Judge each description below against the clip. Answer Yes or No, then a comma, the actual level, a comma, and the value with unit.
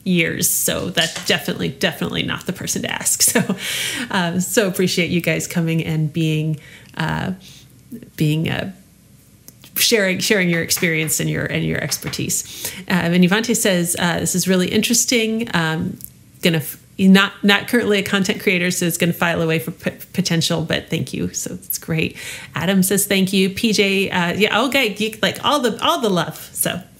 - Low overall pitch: No, medium, 185 Hz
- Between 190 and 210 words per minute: No, average, 175 wpm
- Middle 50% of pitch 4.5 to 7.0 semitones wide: No, average, 3.7 semitones